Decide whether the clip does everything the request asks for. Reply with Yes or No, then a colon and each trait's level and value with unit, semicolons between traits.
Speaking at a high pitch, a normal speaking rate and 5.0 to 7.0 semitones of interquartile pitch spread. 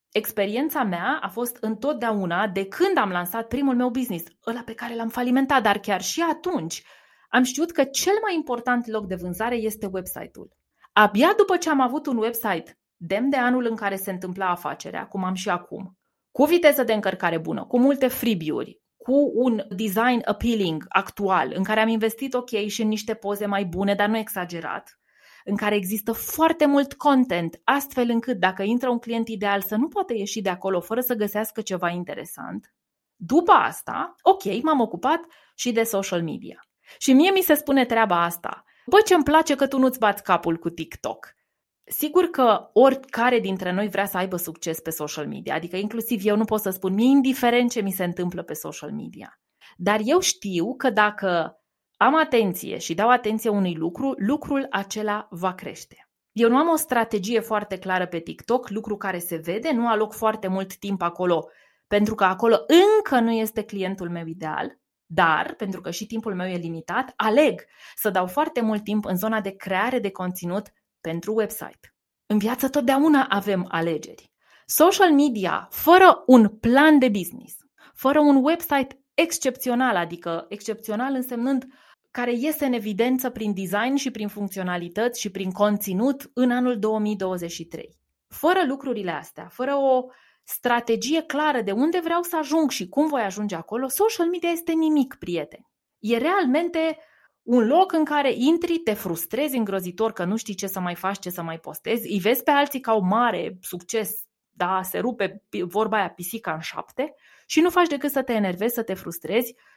No: high, 225 Hz; fast, 180 wpm; wide, 5.6 semitones